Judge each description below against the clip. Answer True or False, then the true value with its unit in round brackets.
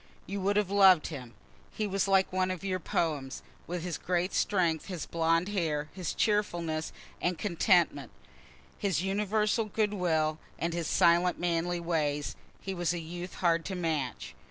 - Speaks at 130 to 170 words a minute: True (160 wpm)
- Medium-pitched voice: True (175 Hz)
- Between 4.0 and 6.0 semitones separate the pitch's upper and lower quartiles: False (2.9 semitones)